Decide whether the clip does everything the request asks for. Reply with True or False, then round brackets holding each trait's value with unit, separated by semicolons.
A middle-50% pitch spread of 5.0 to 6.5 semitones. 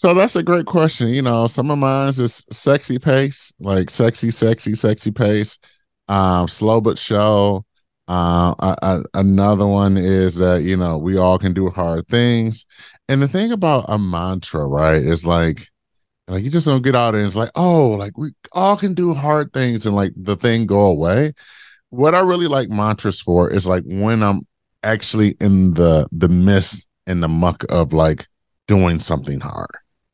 True (5.4 semitones)